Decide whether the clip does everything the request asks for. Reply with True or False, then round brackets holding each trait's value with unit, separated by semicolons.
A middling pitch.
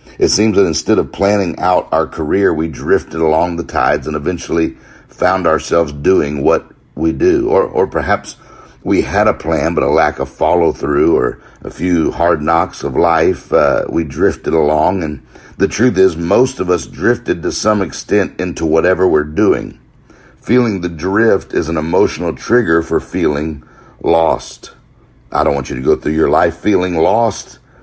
False (90 Hz)